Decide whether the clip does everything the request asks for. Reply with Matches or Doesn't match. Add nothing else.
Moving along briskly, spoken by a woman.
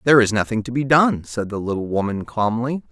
Doesn't match